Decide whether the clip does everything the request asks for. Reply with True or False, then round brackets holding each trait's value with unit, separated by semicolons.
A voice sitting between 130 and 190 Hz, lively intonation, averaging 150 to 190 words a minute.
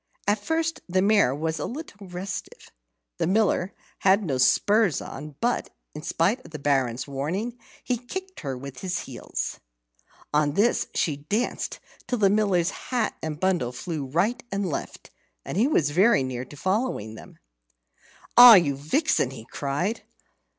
True (185 Hz; 7.0 semitones; 155 wpm)